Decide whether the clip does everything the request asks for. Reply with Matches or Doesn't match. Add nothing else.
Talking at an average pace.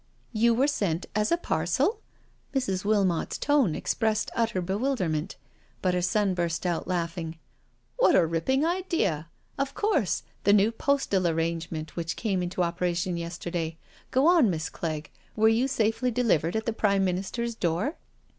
Matches